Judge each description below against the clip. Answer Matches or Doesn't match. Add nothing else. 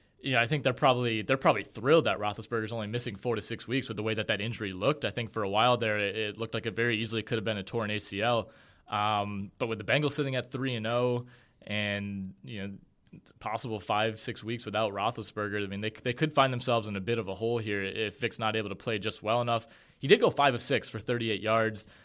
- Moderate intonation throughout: Doesn't match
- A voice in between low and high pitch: Doesn't match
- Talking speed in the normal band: Doesn't match